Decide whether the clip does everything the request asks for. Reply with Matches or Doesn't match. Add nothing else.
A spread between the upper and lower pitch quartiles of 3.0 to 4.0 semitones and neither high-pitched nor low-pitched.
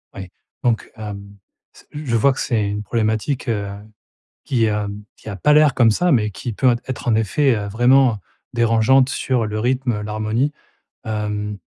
Doesn't match